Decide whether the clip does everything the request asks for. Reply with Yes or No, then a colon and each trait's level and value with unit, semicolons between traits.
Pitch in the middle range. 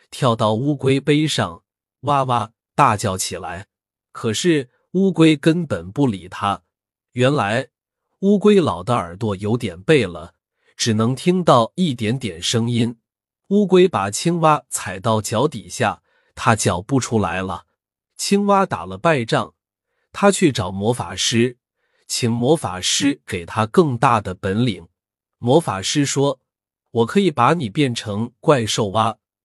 No: low, 120 Hz